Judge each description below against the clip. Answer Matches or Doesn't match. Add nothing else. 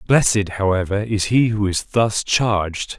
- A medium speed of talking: Matches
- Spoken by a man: Matches